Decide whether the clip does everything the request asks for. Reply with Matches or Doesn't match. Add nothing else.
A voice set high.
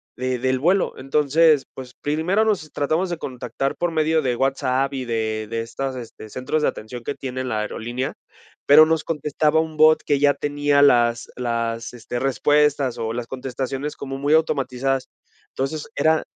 Doesn't match